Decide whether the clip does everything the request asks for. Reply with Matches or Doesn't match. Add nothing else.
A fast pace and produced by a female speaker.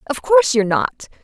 Doesn't match